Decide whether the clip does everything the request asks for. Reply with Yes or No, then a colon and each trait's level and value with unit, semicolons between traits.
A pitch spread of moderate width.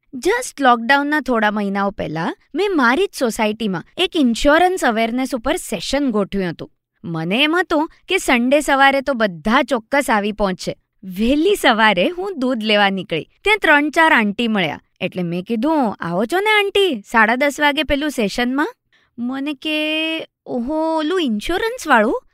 No: wide, 6.3 semitones